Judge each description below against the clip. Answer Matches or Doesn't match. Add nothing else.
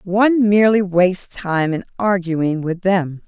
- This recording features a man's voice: Doesn't match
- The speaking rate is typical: Matches